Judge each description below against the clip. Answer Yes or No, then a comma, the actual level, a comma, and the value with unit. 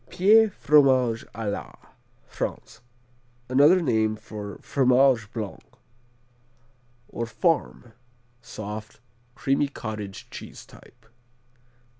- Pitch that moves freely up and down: No, average, 4.6 semitones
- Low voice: Yes, low, 120 Hz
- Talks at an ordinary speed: No, slow, 85 wpm